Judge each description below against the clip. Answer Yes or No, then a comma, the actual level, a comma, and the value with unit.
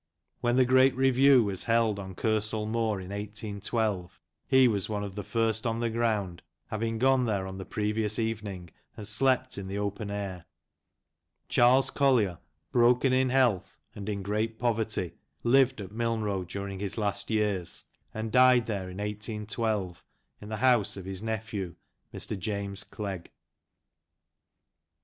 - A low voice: Yes, low, 110 Hz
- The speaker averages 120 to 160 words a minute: Yes, average, 155 wpm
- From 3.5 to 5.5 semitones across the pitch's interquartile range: No, average, 2.9 semitones